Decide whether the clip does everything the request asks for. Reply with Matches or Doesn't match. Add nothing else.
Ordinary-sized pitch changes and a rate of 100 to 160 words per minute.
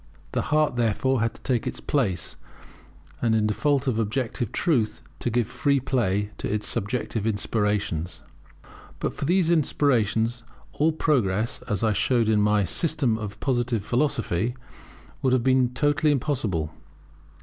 Matches